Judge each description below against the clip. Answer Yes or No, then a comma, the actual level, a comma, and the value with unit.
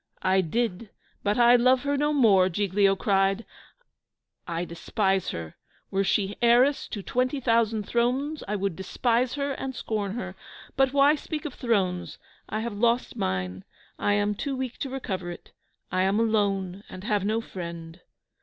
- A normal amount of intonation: Yes, average, 4.5 semitones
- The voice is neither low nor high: No, high, 210 Hz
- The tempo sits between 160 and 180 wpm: Yes, average, 165 wpm